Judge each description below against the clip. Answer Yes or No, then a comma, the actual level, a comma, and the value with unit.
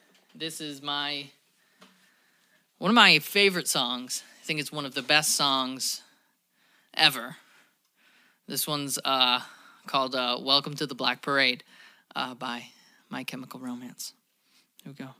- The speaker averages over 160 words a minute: No, average, 140 wpm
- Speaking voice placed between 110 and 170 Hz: Yes, medium, 140 Hz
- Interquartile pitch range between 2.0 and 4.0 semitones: Yes, narrow, 2.6 semitones